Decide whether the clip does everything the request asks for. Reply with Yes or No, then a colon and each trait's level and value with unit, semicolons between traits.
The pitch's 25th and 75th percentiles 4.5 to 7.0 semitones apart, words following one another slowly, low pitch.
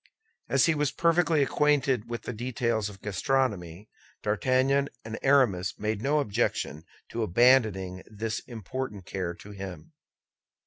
Yes: average, 5.1 semitones; slow, 130 wpm; low, 115 Hz